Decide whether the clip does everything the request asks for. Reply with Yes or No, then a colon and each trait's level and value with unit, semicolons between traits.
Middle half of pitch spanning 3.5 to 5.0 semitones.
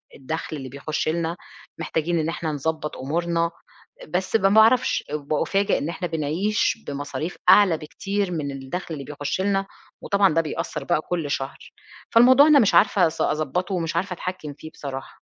Yes: average, 3.9 semitones